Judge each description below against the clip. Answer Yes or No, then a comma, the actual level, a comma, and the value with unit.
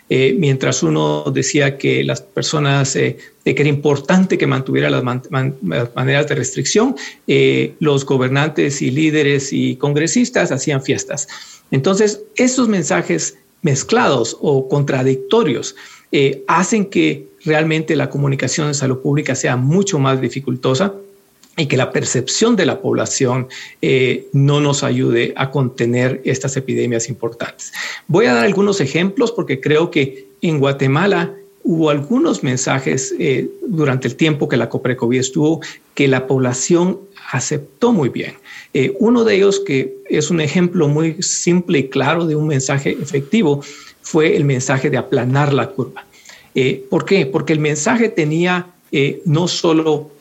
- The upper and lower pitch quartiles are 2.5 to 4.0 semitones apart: No, average, 4.7 semitones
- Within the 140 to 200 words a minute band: Yes, average, 150 wpm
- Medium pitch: Yes, medium, 145 Hz